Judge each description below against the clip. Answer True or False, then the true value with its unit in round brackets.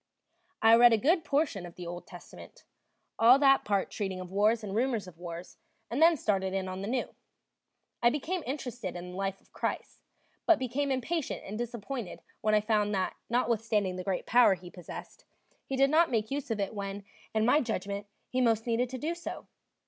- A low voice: False (220 Hz)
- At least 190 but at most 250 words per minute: True (200 wpm)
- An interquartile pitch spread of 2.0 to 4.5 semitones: False (4.9 semitones)